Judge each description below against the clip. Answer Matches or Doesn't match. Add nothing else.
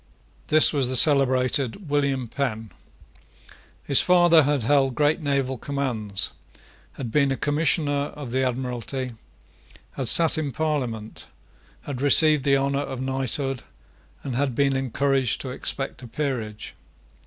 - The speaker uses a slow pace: Matches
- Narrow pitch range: Matches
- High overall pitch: Doesn't match